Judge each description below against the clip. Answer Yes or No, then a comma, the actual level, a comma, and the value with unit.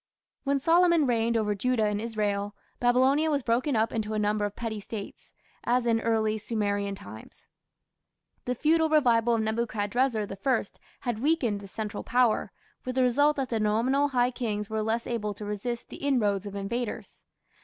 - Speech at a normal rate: Yes, average, 170 wpm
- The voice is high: Yes, high, 230 Hz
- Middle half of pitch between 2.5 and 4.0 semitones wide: Yes, average, 3.3 semitones